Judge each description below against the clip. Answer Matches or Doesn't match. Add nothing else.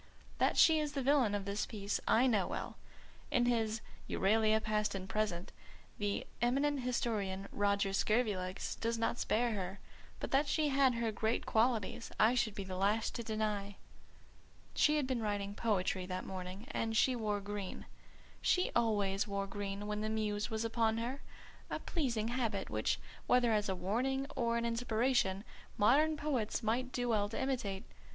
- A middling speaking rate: Matches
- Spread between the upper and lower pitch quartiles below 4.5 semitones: Matches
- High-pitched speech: Matches